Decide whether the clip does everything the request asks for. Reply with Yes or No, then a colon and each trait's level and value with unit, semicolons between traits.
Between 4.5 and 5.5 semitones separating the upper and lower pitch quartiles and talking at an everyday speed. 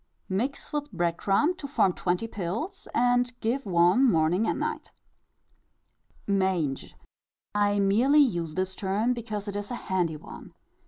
Yes: average, 5.2 semitones; average, 150 wpm